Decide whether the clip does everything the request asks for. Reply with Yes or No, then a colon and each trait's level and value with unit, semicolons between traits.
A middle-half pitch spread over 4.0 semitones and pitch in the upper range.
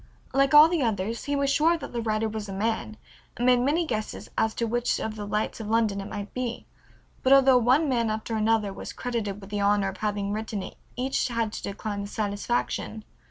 No: average, 3.2 semitones; high, 220 Hz